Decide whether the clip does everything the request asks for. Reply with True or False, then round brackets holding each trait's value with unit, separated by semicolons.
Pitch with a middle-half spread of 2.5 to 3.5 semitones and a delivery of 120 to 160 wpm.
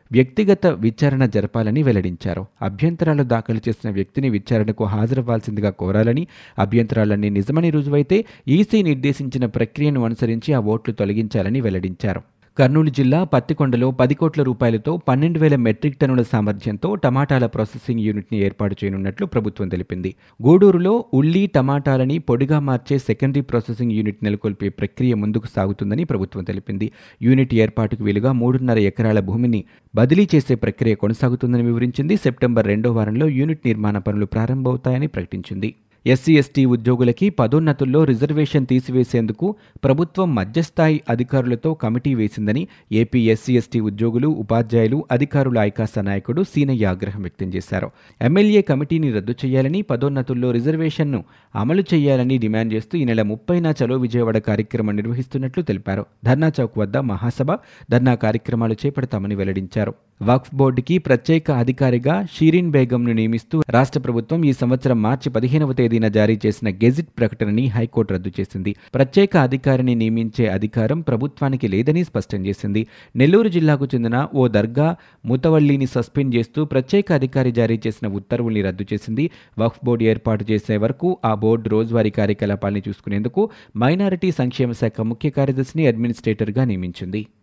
False (4.5 semitones; 125 wpm)